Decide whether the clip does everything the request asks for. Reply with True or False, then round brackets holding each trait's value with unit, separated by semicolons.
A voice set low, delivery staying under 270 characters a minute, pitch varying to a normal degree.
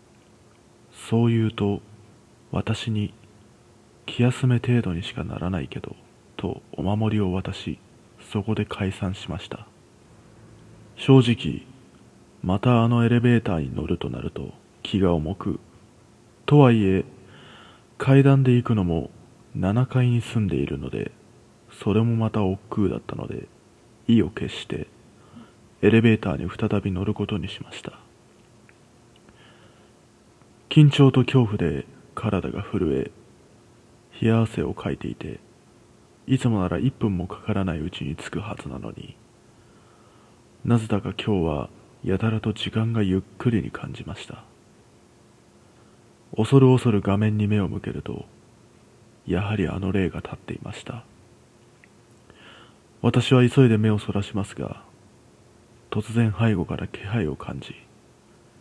True (110 Hz; 240 characters per minute; 3.6 semitones)